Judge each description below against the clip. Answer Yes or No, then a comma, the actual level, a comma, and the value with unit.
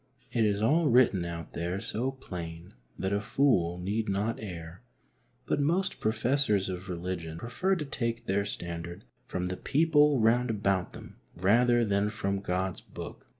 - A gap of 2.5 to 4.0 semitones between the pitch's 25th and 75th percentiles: No, average, 5.2 semitones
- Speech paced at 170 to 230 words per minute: No, average, 155 wpm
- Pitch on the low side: Yes, low, 100 Hz